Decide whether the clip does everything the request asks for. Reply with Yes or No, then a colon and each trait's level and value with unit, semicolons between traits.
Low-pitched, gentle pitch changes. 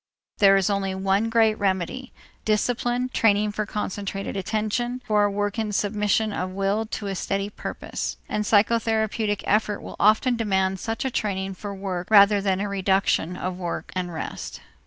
No: high, 205 Hz; narrow, 2.0 semitones